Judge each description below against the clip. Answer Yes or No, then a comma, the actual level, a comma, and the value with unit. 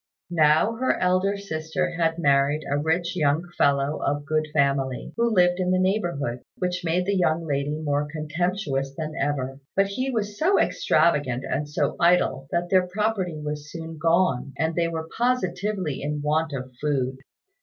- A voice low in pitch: No, medium, 160 Hz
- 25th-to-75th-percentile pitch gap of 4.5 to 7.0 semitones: No, average, 4.0 semitones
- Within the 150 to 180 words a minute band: Yes, average, 165 wpm